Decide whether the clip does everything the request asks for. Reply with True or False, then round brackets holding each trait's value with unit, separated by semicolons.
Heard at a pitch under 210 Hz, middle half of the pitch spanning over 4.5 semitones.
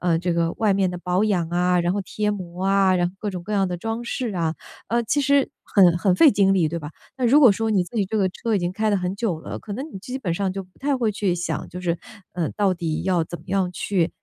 False (190 Hz; 3.2 semitones)